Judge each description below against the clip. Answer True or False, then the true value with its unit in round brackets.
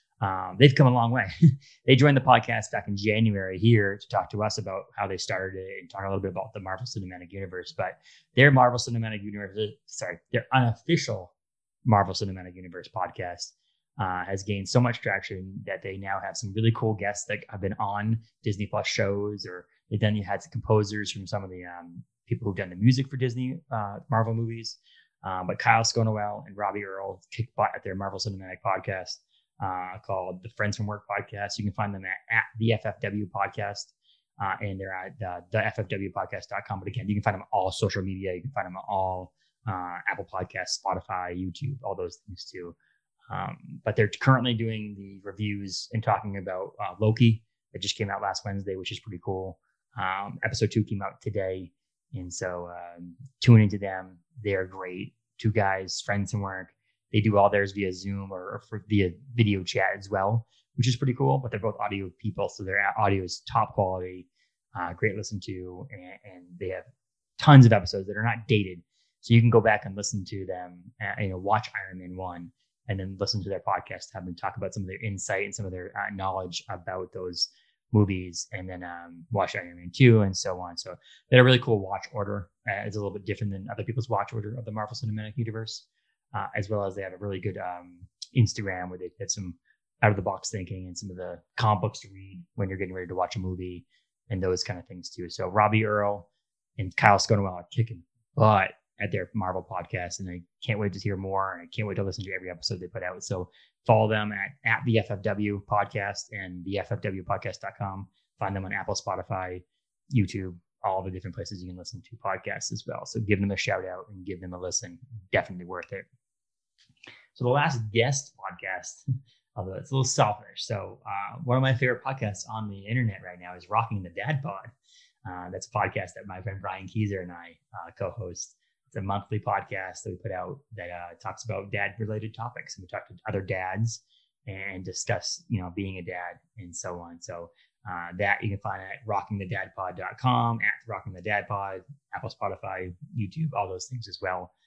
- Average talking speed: False (215 wpm)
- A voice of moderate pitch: False (100 Hz)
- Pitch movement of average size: True (3.1 semitones)